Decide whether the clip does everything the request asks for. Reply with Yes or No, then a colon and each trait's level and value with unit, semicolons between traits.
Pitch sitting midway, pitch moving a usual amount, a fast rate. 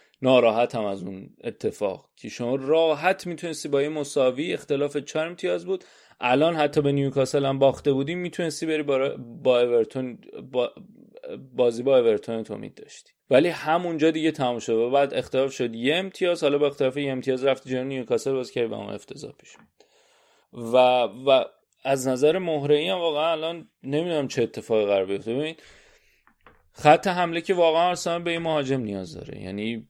Yes: medium, 145 Hz; average, 4.6 semitones; fast, 175 wpm